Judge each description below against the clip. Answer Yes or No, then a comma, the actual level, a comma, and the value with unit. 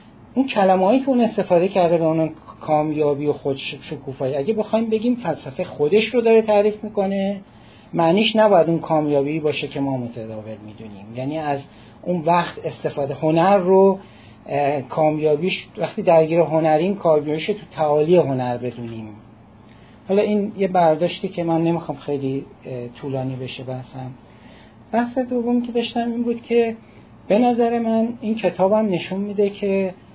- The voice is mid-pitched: Yes, medium, 160 Hz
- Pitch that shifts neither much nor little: No, wide, 6.9 semitones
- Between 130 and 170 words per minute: Yes, average, 140 wpm